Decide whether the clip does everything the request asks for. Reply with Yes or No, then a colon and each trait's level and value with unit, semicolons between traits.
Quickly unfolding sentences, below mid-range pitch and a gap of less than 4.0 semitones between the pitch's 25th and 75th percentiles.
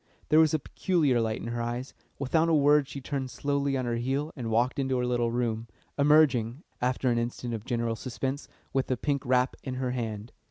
Yes: fast, 210 wpm; low, 130 Hz; average, 3.0 semitones